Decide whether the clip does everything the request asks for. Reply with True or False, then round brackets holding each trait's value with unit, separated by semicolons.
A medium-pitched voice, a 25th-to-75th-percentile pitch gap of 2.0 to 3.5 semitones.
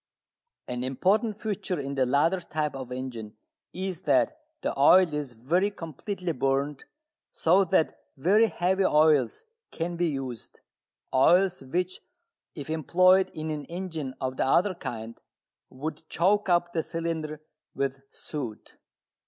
False (160 Hz; 5.2 semitones)